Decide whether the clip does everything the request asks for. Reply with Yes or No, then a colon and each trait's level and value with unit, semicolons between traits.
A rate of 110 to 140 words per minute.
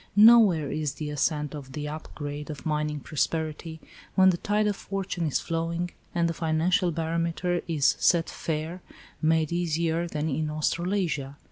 No: average, 155 wpm